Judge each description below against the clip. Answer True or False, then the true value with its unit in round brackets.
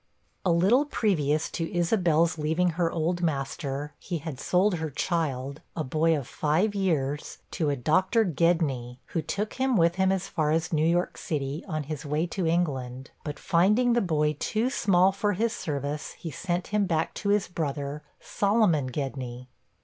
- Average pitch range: True (4.1 semitones)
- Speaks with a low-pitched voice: False (165 Hz)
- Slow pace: False (170 wpm)